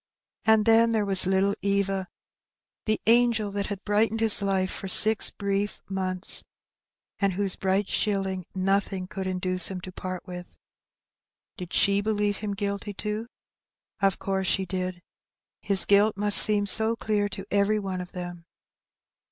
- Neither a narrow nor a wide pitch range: No, narrow, 1.7 semitones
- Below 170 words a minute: Yes, average, 150 wpm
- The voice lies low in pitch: No, high, 200 Hz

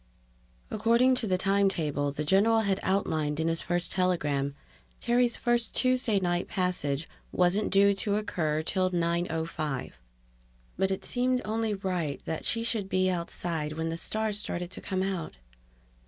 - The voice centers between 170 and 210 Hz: Yes, medium, 185 Hz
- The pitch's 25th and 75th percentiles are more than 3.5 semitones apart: Yes, average, 4.4 semitones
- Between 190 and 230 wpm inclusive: No, average, 155 wpm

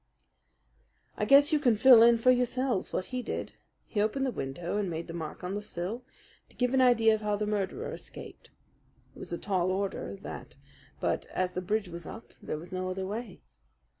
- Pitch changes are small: No, average, 5.0 semitones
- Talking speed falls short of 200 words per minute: No, fast, 205 wpm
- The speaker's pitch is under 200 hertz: No, high, 210 Hz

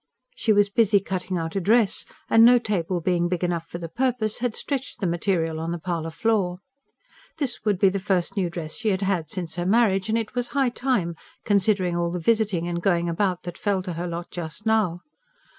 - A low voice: No, high, 190 Hz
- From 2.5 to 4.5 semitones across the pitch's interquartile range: Yes, average, 4.1 semitones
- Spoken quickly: Yes, fast, 215 wpm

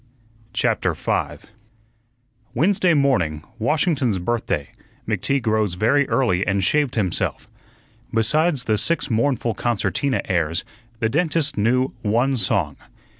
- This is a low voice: Yes, low, 120 Hz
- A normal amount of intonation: No, wide, 5.9 semitones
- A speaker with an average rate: No, slow, 110 wpm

